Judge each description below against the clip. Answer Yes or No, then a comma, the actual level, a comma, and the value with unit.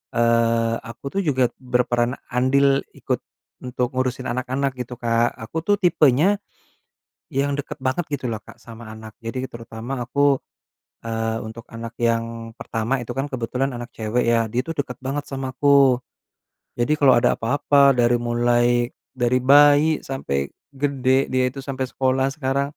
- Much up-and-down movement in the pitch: No, average, 2.7 semitones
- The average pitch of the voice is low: Yes, low, 125 Hz